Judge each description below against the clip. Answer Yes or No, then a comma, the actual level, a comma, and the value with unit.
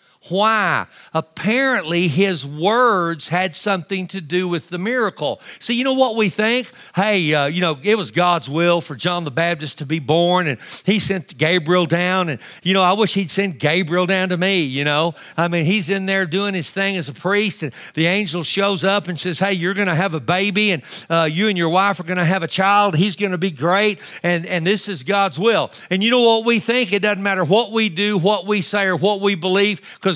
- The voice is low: No, high, 190 Hz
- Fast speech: Yes, fast, 235 wpm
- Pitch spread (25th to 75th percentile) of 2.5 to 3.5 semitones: Yes, average, 2.8 semitones